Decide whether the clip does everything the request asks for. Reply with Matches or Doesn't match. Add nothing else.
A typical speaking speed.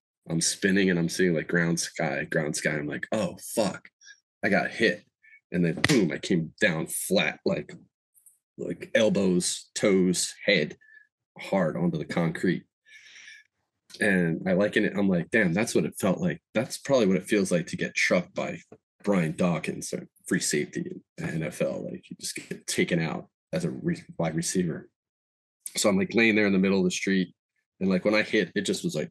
Matches